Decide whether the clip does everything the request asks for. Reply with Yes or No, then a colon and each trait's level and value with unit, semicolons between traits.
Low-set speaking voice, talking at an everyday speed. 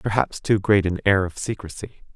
Yes: low, 100 Hz; average, 195 wpm